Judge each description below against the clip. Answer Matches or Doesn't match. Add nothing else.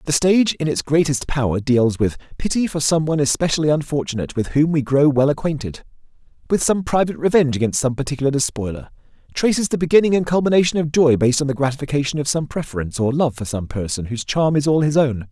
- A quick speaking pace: Matches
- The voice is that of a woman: Doesn't match